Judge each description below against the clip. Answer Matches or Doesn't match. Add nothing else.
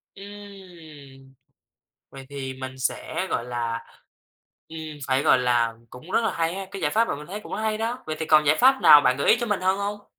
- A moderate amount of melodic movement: Doesn't match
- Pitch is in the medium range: Matches